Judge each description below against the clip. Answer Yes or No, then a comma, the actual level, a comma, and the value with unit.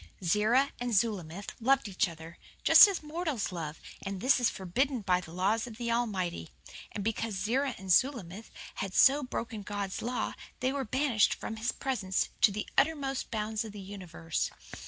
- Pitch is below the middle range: No, high, 220 Hz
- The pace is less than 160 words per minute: No, average, 175 wpm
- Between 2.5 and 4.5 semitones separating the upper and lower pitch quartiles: No, average, 5.0 semitones